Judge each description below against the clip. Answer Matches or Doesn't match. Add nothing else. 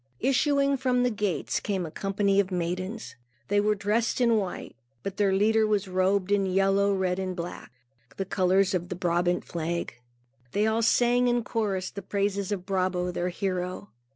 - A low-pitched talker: Doesn't match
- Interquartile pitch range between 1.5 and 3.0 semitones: Matches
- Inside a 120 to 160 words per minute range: Doesn't match